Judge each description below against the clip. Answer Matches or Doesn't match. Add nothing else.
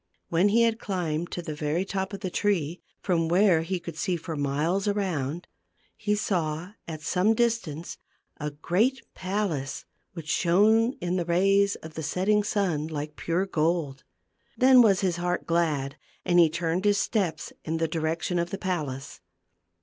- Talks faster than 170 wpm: Doesn't match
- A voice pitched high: Doesn't match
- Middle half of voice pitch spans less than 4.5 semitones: Matches